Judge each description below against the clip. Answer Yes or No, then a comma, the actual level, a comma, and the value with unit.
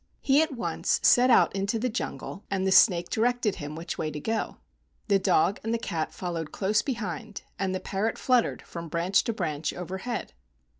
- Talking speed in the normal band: Yes, average, 190 wpm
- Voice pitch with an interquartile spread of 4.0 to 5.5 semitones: Yes, average, 4.9 semitones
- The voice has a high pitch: Yes, high, 195 Hz